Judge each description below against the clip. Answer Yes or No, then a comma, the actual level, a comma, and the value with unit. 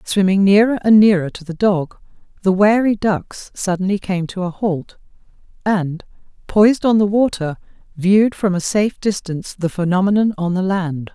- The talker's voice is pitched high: Yes, high, 195 Hz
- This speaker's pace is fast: No, average, 160 wpm